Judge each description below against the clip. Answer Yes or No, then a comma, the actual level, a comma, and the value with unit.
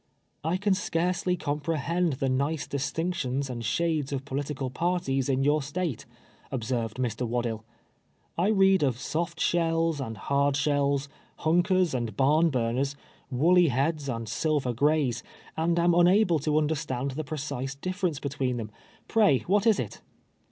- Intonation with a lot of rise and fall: No, average, 4.3 semitones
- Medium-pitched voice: Yes, medium, 145 Hz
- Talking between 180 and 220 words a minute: No, average, 150 wpm